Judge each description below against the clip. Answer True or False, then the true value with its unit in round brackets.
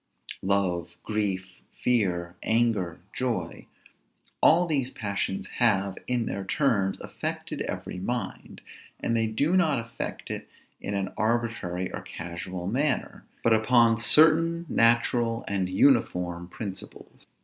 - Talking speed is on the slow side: True (115 wpm)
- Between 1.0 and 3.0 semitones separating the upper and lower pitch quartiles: False (4.4 semitones)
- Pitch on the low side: True (110 Hz)